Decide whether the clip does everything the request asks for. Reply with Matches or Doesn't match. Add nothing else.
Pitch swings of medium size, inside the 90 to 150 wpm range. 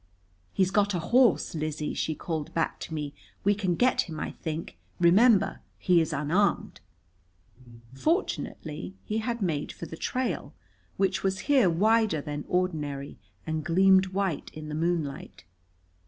Matches